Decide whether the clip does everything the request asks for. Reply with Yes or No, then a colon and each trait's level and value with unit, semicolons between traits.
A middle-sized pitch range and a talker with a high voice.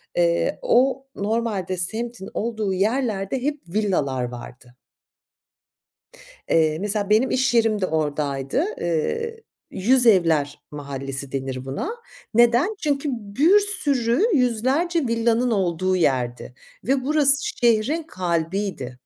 No: wide, 8.4 semitones; high, 215 Hz